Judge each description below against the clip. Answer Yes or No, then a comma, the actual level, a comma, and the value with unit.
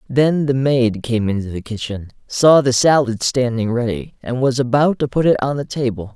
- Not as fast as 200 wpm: No, fast, 205 wpm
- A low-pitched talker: Yes, low, 125 Hz